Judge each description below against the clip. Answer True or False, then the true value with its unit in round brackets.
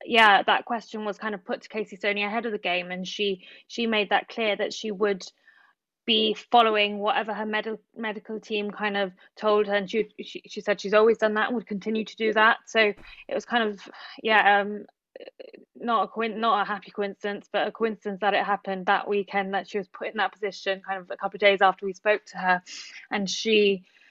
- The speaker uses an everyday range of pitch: False (1.6 semitones)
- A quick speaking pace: True (225 wpm)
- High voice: True (210 Hz)